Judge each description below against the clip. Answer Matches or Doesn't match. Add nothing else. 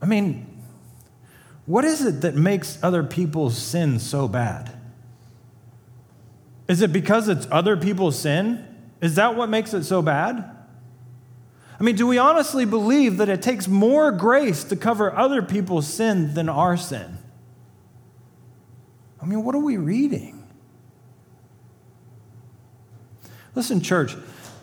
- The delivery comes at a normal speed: Doesn't match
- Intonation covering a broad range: Matches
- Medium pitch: Matches